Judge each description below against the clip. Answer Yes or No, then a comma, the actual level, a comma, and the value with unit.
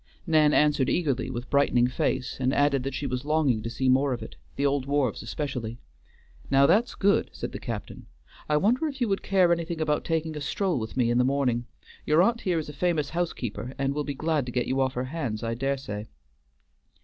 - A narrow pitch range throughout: No, average, 3.9 semitones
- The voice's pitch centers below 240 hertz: Yes, medium, 140 Hz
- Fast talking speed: Yes, fast, 220 wpm